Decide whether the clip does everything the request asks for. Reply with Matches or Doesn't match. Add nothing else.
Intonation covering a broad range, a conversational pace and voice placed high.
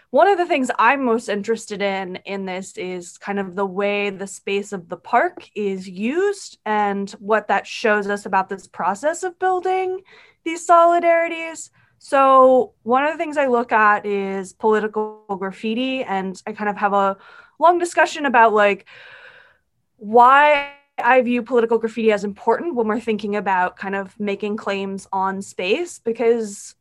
Matches